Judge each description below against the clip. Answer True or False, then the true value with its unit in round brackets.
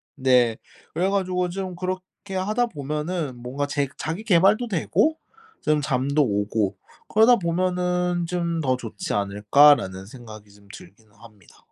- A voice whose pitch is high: False (150 Hz)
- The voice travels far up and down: True (7.4 semitones)